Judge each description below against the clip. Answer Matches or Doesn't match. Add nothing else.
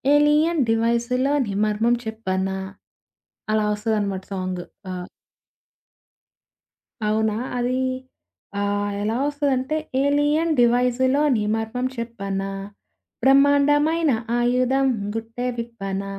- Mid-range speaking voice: Doesn't match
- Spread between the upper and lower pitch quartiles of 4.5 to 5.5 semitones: Matches